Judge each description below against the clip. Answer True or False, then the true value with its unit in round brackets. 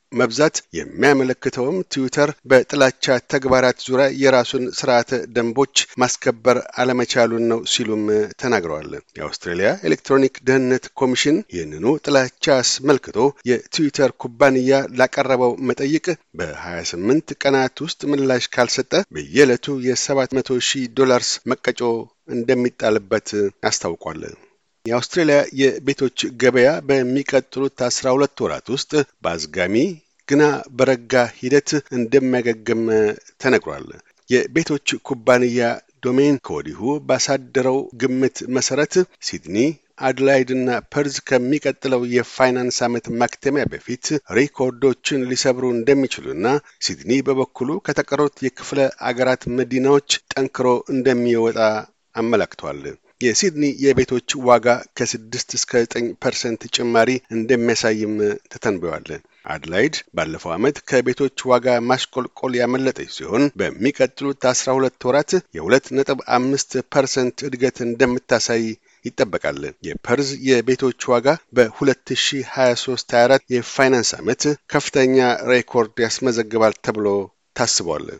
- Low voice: True (130 Hz)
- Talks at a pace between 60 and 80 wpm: False (95 wpm)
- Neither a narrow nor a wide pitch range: False (2.0 semitones)